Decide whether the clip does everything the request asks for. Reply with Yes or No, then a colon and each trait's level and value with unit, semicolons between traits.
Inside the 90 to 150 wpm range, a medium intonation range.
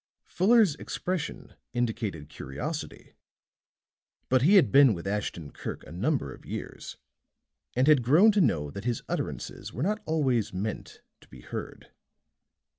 No: average, 140 wpm; wide, 8.4 semitones